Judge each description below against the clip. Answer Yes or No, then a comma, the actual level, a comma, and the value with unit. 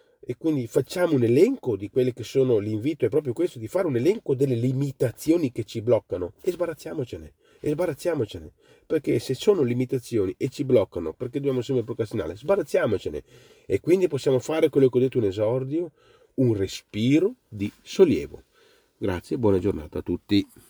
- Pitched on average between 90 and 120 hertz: No, low, 130 Hz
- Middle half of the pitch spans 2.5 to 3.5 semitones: No, average, 5.3 semitones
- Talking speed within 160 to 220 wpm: Yes, fast, 170 wpm